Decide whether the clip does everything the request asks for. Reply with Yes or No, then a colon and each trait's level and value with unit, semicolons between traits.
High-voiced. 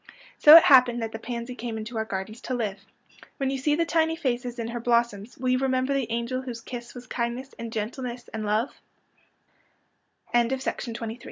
Yes: high, 240 Hz